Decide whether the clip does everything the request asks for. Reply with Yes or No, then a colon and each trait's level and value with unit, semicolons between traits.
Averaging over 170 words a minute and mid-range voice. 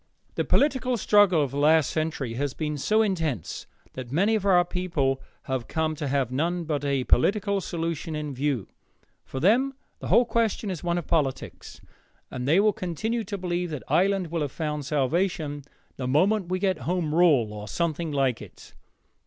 Yes: average, 180 wpm; medium, 160 Hz